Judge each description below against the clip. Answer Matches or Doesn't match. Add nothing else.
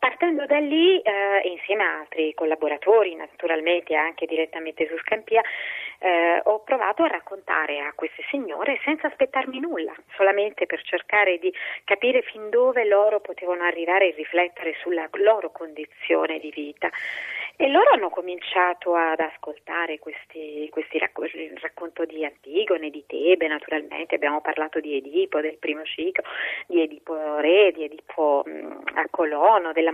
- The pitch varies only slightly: Doesn't match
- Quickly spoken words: Doesn't match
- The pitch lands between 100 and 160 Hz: Doesn't match